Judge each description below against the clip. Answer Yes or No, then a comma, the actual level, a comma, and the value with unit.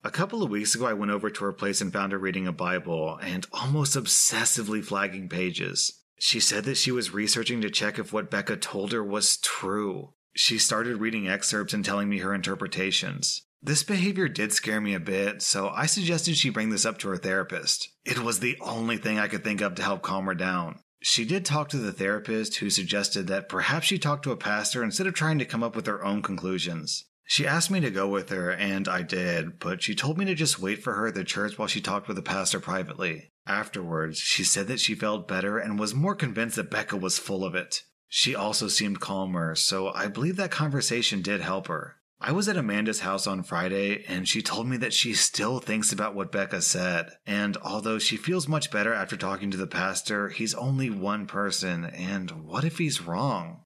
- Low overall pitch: Yes, low, 105 Hz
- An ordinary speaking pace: No, fast, 225 wpm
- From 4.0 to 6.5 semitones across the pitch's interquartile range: Yes, average, 4.7 semitones